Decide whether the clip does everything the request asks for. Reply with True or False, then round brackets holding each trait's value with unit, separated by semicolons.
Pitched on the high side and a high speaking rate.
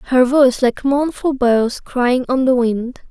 False (255 Hz; 175 wpm)